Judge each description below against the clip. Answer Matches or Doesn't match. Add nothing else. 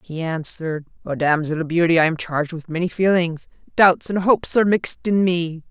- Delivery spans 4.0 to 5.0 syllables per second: Doesn't match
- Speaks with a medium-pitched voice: Matches